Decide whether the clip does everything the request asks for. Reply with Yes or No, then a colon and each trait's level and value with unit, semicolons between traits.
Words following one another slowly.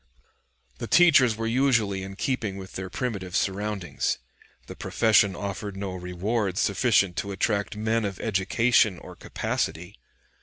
Yes: slow, 130 wpm